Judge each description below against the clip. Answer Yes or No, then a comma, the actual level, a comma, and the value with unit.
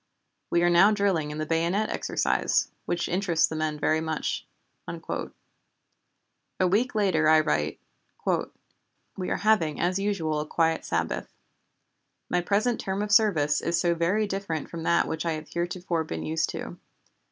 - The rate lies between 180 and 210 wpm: No, average, 155 wpm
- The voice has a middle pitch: Yes, medium, 170 Hz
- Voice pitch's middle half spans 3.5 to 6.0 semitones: Yes, average, 3.8 semitones